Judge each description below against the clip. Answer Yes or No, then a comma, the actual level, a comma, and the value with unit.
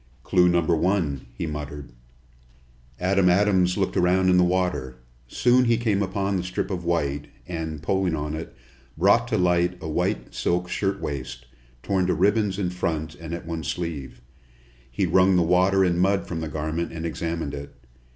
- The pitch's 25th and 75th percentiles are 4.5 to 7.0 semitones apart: No, average, 2.9 semitones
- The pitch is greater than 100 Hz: No, very low, 90 Hz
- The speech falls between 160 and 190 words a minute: Yes, average, 170 wpm